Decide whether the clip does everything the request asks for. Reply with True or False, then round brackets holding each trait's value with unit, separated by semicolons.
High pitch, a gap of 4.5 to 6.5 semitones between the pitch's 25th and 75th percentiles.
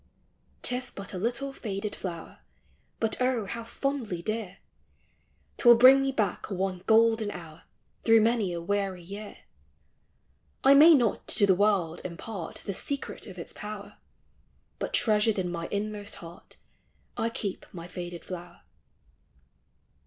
False (205 Hz; 4.0 semitones)